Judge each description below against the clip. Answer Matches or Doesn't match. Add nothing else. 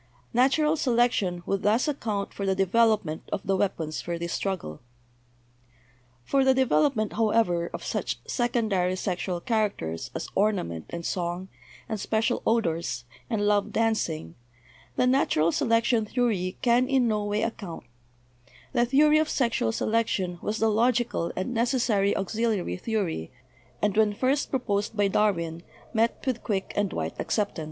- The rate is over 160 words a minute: Doesn't match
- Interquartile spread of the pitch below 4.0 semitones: Doesn't match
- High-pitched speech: Matches